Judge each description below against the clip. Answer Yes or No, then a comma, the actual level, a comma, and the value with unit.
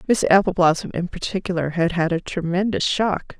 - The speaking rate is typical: Yes, average, 160 wpm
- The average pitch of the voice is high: No, medium, 180 Hz